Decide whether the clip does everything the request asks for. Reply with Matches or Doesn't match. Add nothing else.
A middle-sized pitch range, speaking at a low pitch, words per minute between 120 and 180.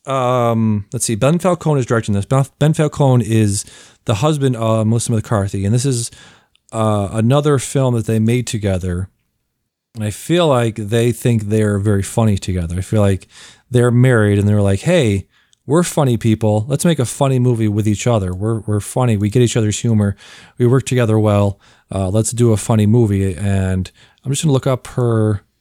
Doesn't match